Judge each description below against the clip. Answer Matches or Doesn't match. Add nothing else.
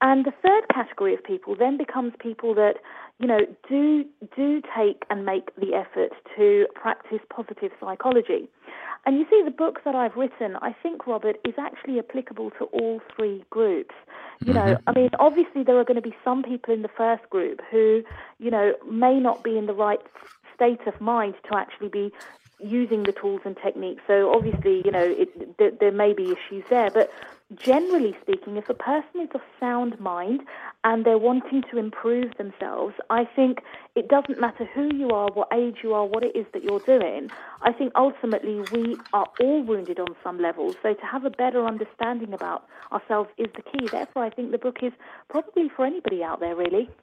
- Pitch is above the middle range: Matches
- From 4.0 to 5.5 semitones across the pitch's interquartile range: Matches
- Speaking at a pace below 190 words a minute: Doesn't match